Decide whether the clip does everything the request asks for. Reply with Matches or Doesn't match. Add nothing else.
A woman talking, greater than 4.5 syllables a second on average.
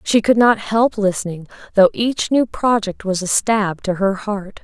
Doesn't match